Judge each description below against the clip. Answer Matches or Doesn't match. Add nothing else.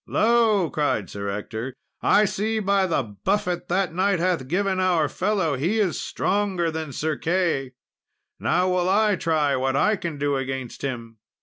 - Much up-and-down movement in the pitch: Matches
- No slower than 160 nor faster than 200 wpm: Matches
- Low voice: Doesn't match